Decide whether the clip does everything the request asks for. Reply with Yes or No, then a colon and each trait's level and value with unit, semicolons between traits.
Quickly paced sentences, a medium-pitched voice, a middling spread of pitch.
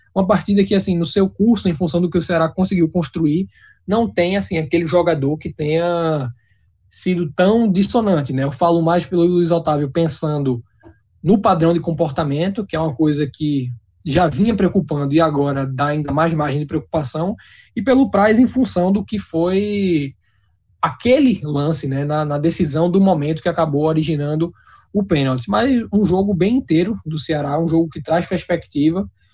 No: average, 175 wpm; medium, 165 Hz; average, 3.9 semitones